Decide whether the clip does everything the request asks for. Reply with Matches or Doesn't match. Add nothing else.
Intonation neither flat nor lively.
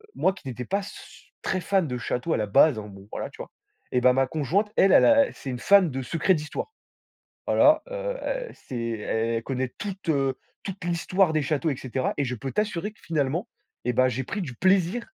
Doesn't match